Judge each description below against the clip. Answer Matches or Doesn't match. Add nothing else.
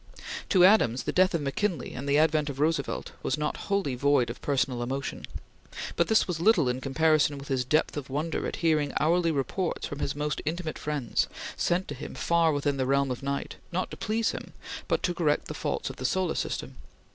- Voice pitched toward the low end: Doesn't match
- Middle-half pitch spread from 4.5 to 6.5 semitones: Doesn't match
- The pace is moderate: Doesn't match